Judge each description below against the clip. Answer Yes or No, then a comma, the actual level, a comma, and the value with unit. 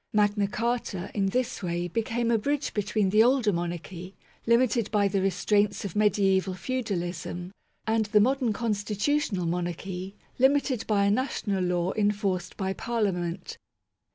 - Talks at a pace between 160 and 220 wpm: No, slow, 135 wpm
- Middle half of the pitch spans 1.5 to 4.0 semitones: Yes, average, 3.5 semitones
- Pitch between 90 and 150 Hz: No, high, 205 Hz